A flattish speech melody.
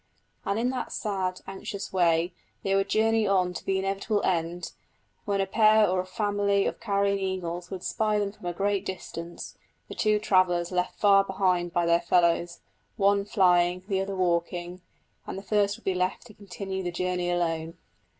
Yes: narrow, 2.2 semitones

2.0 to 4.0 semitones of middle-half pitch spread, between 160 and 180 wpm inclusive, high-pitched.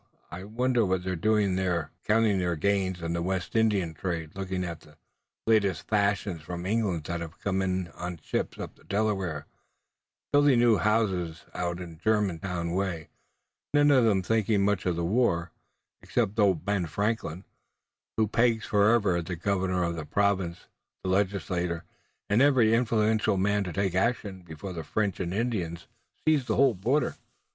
No: average, 3.7 semitones; average, 165 wpm; very low, 95 Hz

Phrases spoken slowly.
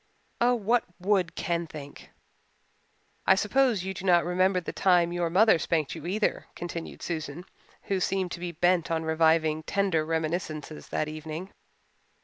No: average, 150 wpm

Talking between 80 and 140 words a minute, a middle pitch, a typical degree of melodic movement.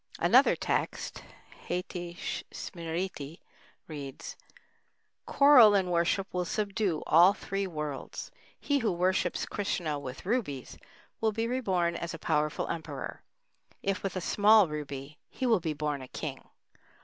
Yes: slow, 135 wpm; medium, 175 Hz; average, 4.9 semitones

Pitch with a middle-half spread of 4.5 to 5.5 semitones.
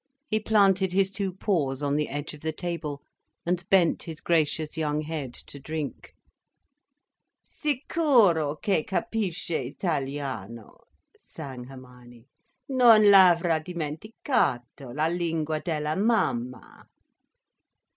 Yes: average, 5.0 semitones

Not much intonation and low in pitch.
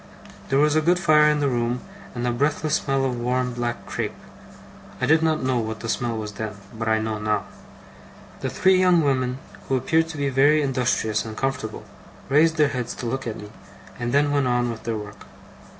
No: average, 4.2 semitones; low, 130 Hz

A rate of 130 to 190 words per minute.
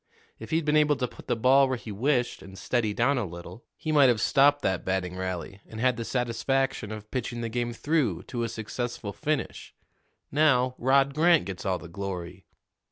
No: average, 200 wpm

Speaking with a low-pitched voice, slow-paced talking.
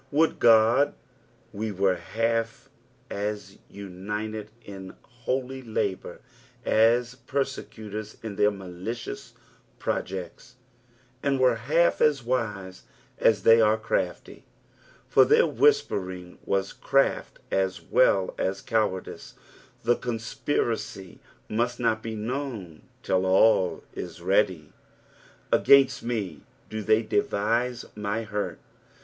Yes: low, 110 Hz; slow, 105 wpm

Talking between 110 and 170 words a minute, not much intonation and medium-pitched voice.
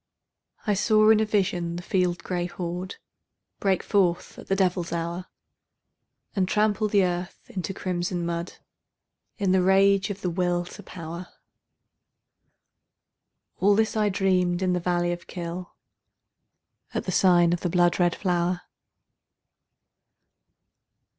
Yes: slow, 135 wpm; narrow, 1.8 semitones; medium, 180 Hz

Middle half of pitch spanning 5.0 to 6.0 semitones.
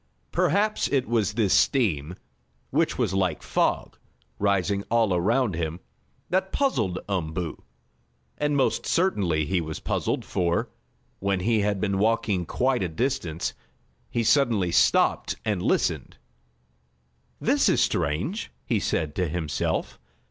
Yes: average, 5.3 semitones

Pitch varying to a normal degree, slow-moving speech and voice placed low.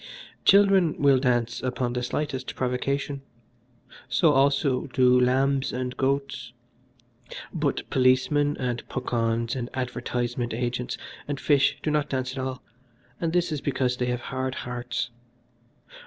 No: narrow, 2.2 semitones; slow, 130 wpm; low, 130 Hz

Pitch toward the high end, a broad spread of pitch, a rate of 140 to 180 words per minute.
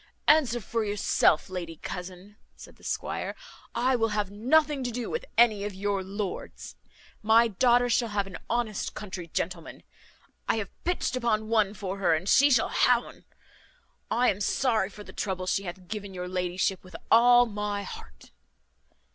No: high, 210 Hz; average, 4.0 semitones; average, 170 wpm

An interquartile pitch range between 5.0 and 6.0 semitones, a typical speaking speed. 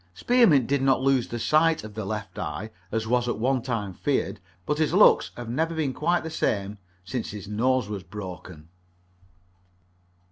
Yes: average, 5.3 semitones; average, 175 wpm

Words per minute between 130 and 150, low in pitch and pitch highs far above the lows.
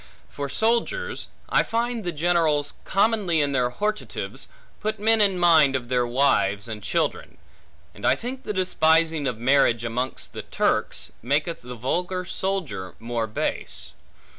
No: average, 145 wpm; medium, 160 Hz; wide, 7.9 semitones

